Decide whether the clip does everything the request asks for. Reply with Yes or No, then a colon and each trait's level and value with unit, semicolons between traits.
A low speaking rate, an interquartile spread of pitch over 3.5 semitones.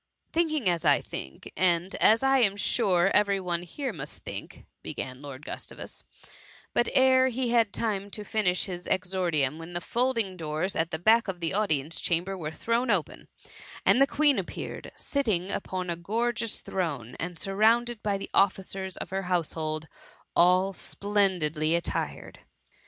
No: average, 165 wpm; average, 4.7 semitones